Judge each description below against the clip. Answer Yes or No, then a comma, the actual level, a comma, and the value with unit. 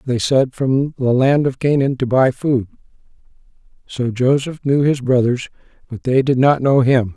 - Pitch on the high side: No, low, 130 Hz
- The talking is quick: No, average, 175 wpm